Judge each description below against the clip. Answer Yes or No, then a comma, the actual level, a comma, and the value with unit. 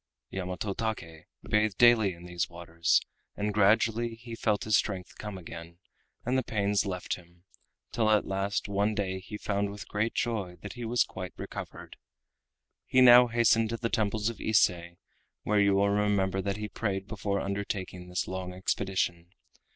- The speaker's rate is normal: Yes, average, 165 wpm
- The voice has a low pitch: Yes, low, 100 Hz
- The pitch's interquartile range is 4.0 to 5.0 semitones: No, average, 2.8 semitones